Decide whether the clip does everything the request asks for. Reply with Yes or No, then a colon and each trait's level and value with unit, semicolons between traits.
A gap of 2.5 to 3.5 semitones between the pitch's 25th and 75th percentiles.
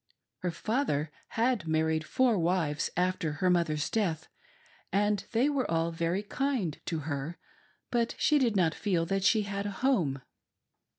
No: wide, 5.5 semitones